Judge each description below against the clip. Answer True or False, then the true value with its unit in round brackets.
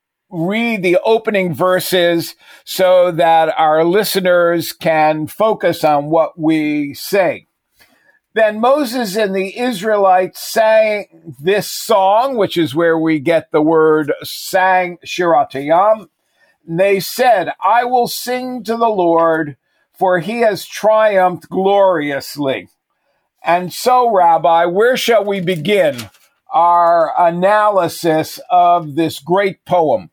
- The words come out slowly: True (115 wpm)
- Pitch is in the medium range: True (180 Hz)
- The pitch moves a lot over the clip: False (4.6 semitones)